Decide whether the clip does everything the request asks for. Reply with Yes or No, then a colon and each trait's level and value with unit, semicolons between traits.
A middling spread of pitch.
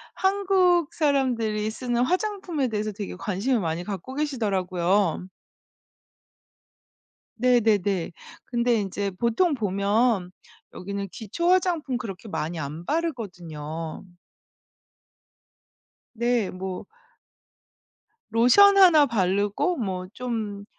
No: wide, 6.0 semitones